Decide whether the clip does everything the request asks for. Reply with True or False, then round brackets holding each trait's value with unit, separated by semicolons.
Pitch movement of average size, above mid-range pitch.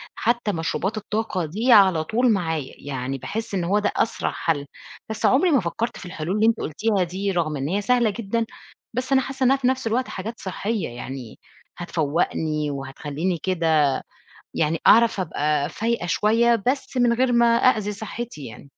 False (6.6 semitones; 200 Hz)